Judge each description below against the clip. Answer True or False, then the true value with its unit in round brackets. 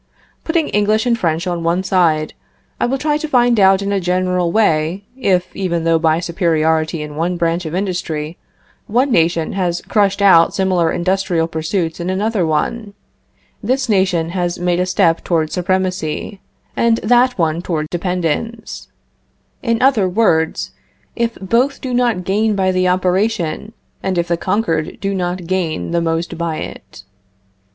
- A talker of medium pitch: True (180 Hz)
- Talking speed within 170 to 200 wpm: False (160 wpm)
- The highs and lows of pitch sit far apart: False (3.7 semitones)